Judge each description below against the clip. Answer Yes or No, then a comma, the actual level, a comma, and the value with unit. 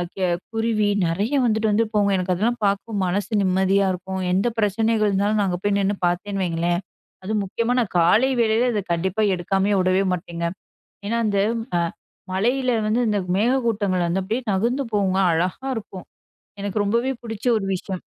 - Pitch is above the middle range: Yes, high, 200 Hz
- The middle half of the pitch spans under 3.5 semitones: Yes, average, 3.0 semitones